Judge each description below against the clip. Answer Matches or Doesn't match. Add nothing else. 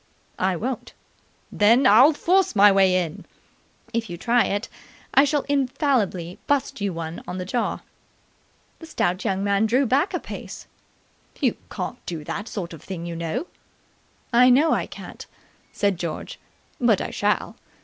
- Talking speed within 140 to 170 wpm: Matches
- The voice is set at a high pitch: Matches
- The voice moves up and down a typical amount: Doesn't match